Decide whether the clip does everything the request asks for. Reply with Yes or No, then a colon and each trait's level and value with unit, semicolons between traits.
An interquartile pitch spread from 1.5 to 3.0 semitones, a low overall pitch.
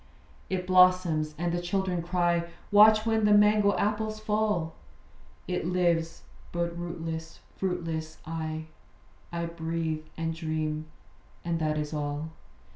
No: narrow, 2.4 semitones; medium, 170 Hz